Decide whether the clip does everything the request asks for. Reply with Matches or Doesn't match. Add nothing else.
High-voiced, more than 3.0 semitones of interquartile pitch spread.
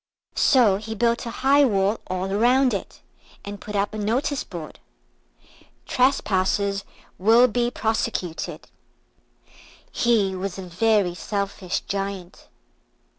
Matches